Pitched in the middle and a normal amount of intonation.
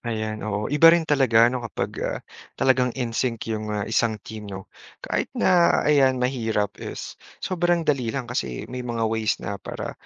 No: low, 120 Hz; average, 3.6 semitones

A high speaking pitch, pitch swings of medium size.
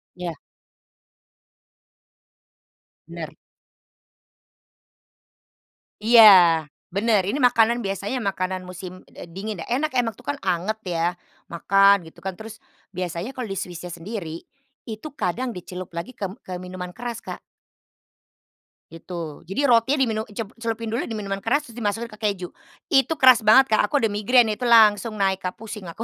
Yes: high, 210 Hz; average, 4.2 semitones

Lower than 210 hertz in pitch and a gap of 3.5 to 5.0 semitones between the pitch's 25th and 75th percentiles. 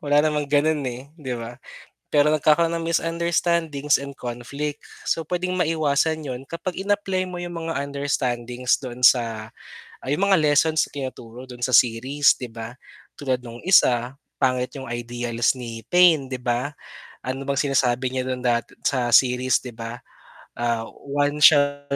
Yes: medium, 140 Hz; average, 4.0 semitones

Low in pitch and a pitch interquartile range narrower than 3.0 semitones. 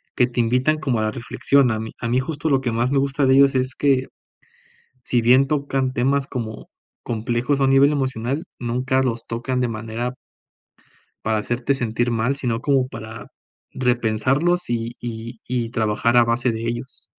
Yes: low, 125 Hz; narrow, 2.5 semitones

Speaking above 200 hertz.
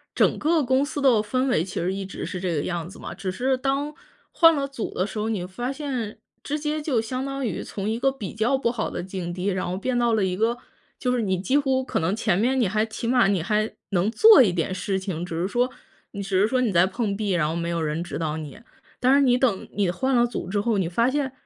Yes: high, 220 Hz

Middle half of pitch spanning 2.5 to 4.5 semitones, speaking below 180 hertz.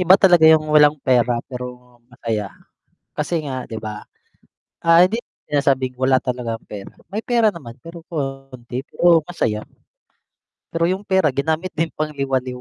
No: average, 4.9 semitones; medium, 140 Hz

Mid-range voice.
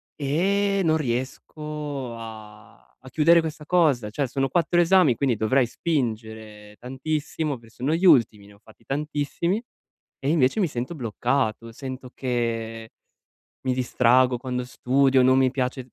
No: low, 130 Hz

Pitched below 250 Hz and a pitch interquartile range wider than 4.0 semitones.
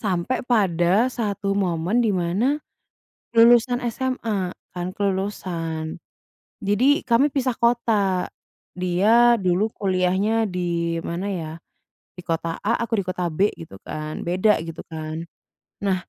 Yes: high, 190 Hz; average, 4.7 semitones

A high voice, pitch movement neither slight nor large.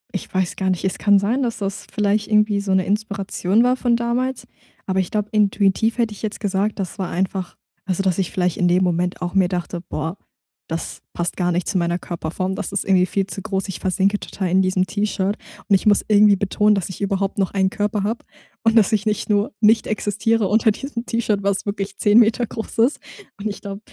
No: high, 200 Hz; narrow, 2.1 semitones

